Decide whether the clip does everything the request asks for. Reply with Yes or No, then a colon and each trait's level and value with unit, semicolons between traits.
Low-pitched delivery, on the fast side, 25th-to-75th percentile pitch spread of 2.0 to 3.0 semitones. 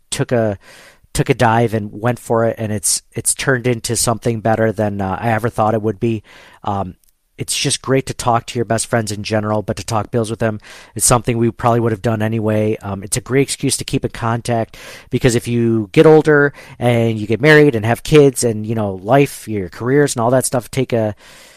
Yes: low, 115 Hz; fast, 230 wpm; narrow, 2.4 semitones